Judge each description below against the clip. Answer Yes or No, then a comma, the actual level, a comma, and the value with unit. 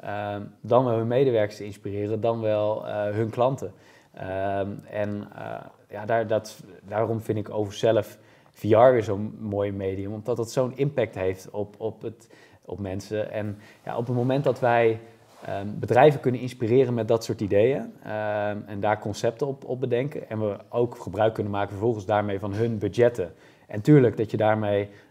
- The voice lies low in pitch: Yes, low, 110 Hz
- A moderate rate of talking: Yes, average, 180 wpm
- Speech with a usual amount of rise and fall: No, narrow, 2.2 semitones